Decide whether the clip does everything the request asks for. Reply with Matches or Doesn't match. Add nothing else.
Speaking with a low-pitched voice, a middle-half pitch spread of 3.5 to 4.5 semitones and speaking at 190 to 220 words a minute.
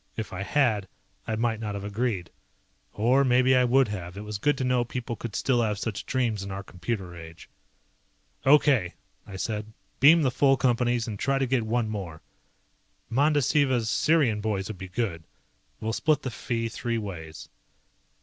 Doesn't match